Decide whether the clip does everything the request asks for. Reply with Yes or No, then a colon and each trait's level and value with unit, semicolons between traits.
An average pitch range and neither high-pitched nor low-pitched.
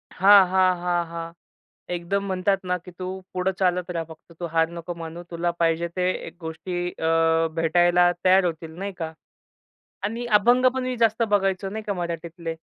No: narrow, 2.3 semitones; medium, 175 Hz